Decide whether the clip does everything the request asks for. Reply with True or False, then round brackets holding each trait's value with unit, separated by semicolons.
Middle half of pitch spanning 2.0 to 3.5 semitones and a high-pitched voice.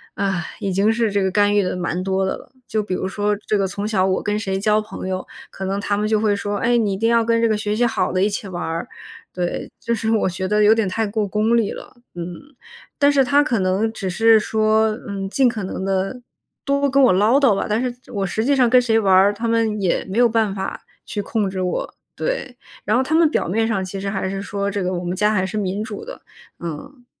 True (2.9 semitones; 210 Hz)